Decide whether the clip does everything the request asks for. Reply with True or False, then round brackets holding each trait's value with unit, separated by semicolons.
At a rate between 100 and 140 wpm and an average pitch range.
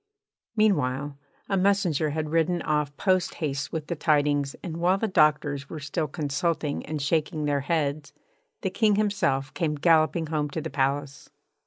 False (155 wpm; 3.2 semitones)